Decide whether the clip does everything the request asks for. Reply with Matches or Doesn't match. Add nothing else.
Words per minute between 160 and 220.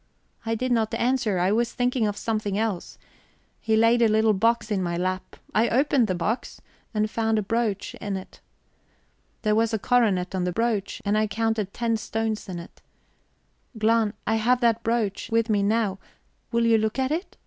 Matches